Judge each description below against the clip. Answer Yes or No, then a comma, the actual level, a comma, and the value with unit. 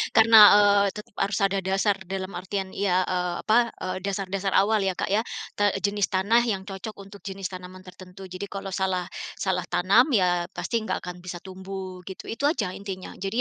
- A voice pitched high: Yes, high, 195 Hz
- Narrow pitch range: Yes, narrow, 1.5 semitones